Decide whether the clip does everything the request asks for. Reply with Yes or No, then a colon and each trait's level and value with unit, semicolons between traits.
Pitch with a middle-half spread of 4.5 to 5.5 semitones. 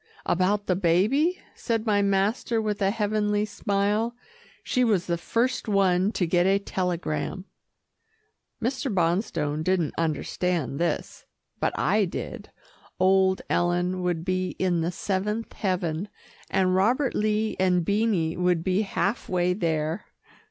No: average, 3.1 semitones